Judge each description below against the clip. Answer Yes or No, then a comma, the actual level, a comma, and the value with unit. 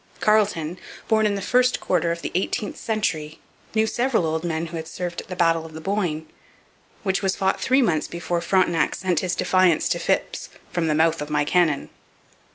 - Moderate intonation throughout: Yes, average, 3.4 semitones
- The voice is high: No, medium, 175 Hz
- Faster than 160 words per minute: Yes, average, 195 wpm